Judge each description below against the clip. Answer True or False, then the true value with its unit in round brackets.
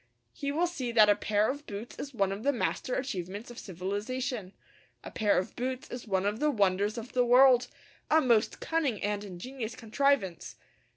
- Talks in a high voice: True (230 Hz)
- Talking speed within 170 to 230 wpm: True (185 wpm)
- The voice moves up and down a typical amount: True (4.3 semitones)